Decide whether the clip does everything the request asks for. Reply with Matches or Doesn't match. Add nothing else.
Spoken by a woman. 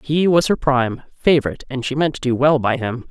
Matches